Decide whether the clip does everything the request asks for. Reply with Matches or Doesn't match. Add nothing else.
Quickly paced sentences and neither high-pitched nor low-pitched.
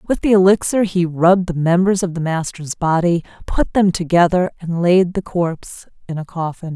Doesn't match